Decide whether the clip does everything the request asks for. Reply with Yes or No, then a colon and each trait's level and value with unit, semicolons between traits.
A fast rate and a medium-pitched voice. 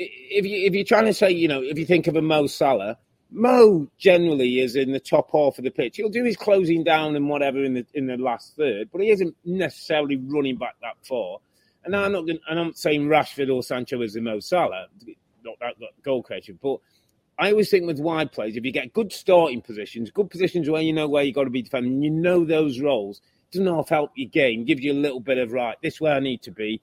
Yes: fast, 255 wpm; medium, 155 Hz